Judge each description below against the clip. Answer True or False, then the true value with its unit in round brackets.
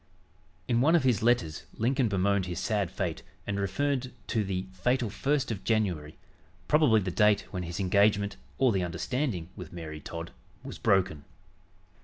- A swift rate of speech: False (160 wpm)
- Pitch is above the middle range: False (100 Hz)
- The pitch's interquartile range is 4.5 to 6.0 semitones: True (5.1 semitones)